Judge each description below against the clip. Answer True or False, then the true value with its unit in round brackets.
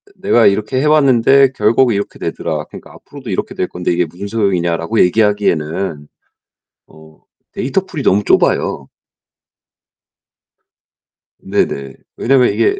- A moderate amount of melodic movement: False (7.1 semitones)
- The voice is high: False (105 Hz)